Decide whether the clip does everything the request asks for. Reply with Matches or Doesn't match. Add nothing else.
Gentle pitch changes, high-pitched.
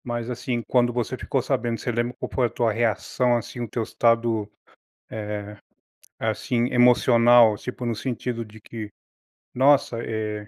Doesn't match